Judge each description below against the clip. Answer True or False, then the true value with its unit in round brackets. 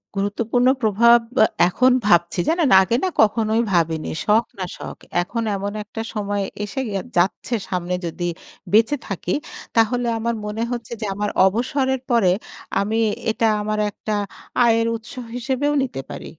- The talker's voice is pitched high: True (220 Hz)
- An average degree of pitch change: True (3.1 semitones)